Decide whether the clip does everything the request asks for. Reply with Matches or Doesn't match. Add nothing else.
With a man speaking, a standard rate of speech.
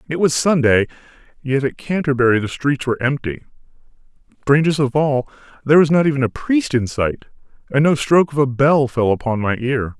Matches